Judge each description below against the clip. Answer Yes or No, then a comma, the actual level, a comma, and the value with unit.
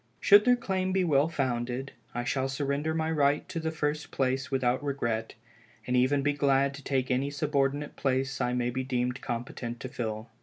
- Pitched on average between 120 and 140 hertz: Yes, low, 135 Hz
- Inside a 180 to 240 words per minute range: Yes, average, 190 wpm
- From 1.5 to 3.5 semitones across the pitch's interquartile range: Yes, average, 2.8 semitones